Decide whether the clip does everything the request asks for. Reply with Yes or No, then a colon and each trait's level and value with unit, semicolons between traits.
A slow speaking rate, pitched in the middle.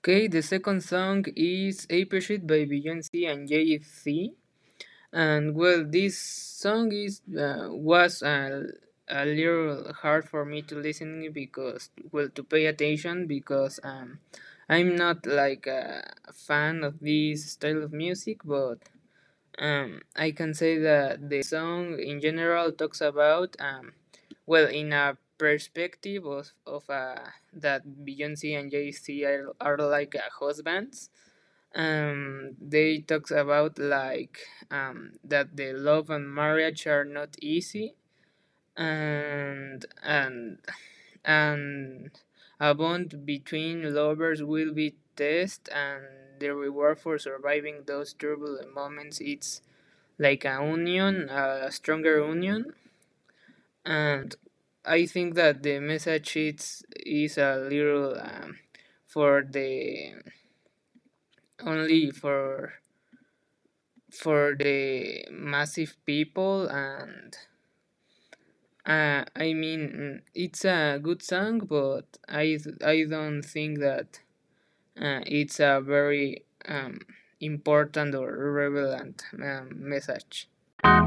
Yes: slow, 115 wpm; medium, 150 Hz